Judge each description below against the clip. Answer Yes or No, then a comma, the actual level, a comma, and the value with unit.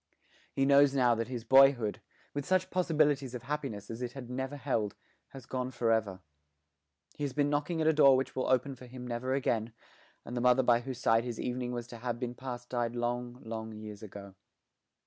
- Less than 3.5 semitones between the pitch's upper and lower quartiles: Yes, narrow, 2.4 semitones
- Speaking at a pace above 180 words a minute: Yes, fast, 205 wpm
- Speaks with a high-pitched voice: No, low, 125 Hz